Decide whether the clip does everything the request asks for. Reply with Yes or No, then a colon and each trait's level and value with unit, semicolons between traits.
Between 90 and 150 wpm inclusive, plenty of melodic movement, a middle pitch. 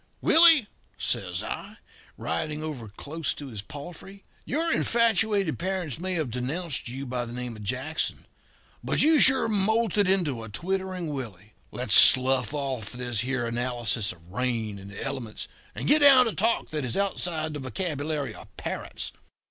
No: average, 165 wpm; wide, 7.7 semitones; medium, 145 Hz